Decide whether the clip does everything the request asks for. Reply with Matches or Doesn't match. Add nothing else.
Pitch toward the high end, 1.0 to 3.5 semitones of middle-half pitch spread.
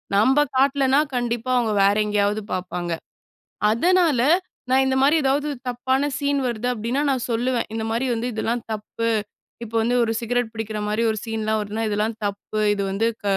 Matches